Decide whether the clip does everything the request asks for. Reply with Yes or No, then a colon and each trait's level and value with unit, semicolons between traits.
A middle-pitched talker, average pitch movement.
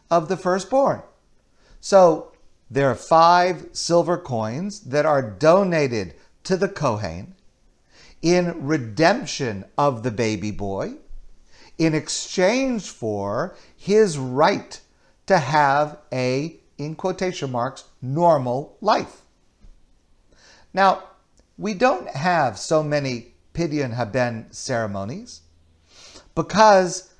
No: medium, 150 Hz; wide, 6.9 semitones